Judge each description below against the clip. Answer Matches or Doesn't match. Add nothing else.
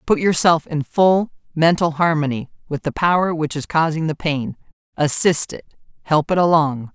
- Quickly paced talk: Doesn't match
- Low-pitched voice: Doesn't match